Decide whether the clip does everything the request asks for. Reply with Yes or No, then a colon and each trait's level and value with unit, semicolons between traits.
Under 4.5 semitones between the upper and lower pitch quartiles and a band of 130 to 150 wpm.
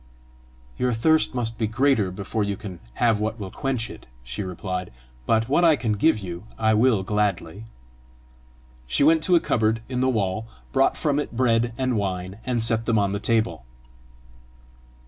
No: average, 3.9 semitones; average, 175 wpm